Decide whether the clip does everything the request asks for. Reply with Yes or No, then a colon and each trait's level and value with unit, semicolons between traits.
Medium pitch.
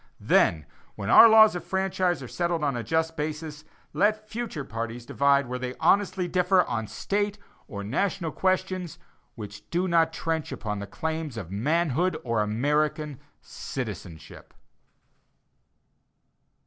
Yes: medium, 155 Hz